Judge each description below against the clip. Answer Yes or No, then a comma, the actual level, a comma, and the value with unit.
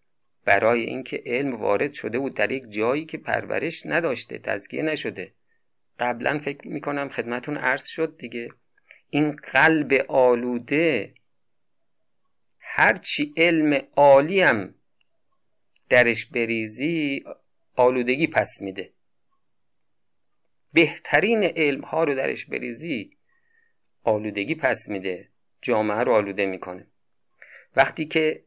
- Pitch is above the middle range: No, low, 135 Hz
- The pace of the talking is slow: Yes, slow, 100 wpm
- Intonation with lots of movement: No, average, 4.7 semitones